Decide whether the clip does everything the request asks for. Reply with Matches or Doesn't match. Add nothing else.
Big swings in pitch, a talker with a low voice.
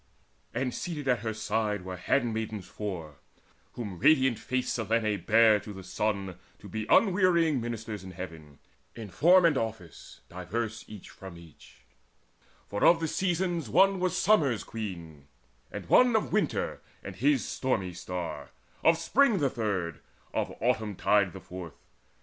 Matches